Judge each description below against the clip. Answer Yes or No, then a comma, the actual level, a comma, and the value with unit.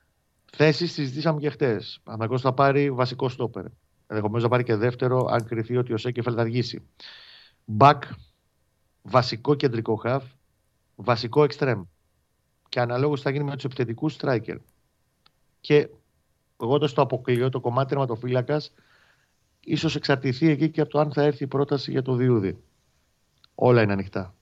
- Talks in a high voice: No, low, 125 Hz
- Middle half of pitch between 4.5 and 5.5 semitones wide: No, average, 3.9 semitones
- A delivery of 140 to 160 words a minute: Yes, average, 145 wpm